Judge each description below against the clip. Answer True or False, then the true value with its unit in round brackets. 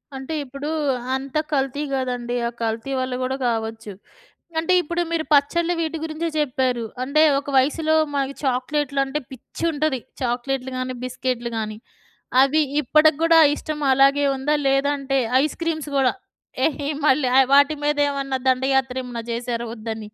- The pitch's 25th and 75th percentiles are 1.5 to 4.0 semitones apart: True (2.9 semitones)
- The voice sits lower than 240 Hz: False (270 Hz)